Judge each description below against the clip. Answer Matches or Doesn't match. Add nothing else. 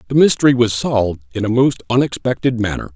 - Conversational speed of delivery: Matches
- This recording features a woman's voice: Doesn't match